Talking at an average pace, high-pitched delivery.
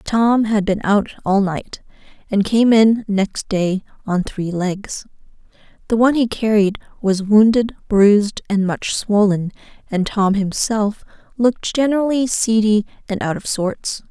Yes: average, 145 wpm; high, 210 Hz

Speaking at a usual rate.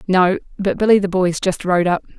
No: fast, 220 wpm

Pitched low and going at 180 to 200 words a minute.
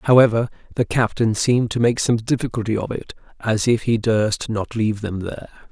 Yes: low, 115 Hz; average, 190 wpm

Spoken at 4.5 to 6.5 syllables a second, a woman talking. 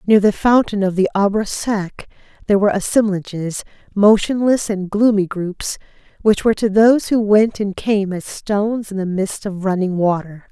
Yes: 4.9 syllables/s; female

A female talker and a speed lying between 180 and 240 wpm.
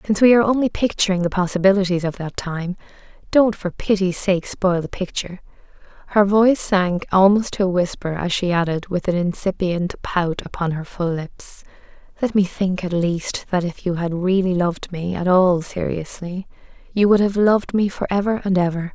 Yes: female; average, 185 wpm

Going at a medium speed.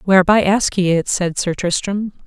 Yes: average, 185 wpm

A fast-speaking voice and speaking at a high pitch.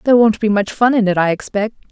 Yes: fast, 280 wpm; high, 215 Hz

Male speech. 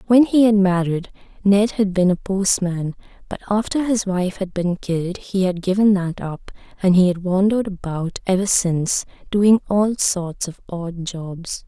No: female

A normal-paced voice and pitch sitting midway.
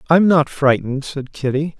Yes: average, 165 wpm; medium, 145 Hz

